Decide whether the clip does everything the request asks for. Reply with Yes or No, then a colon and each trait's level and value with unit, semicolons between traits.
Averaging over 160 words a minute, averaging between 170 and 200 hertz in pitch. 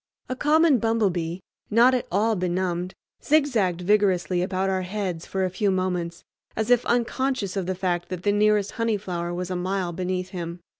Yes: average, 180 wpm; high, 190 Hz